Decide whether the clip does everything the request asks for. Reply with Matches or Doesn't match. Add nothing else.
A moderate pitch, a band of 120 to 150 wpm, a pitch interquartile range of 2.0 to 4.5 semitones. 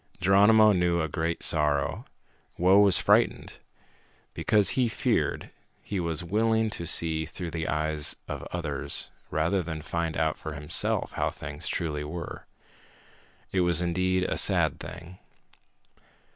Doesn't match